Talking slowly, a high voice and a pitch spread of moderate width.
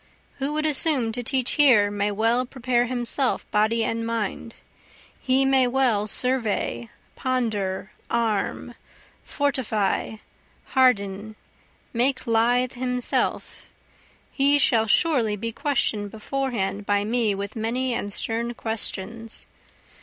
Yes: slow, 110 wpm; high, 230 Hz; average, 3.4 semitones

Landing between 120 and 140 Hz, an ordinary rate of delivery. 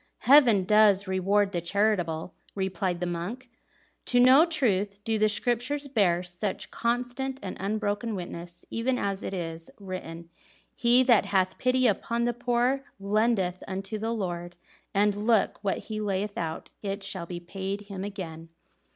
No: high, 205 Hz; average, 150 wpm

